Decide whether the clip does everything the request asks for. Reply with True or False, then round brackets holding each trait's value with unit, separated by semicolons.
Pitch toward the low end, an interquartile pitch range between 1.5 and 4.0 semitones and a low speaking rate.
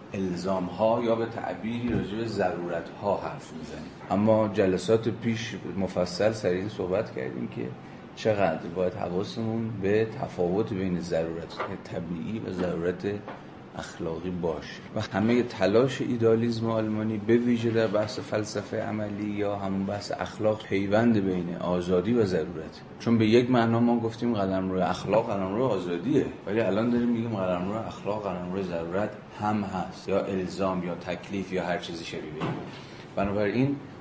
False (100 Hz; 3.7 semitones; 150 wpm)